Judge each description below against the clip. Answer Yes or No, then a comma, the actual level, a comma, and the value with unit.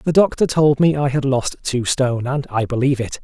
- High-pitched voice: No, low, 135 Hz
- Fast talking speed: Yes, fast, 240 wpm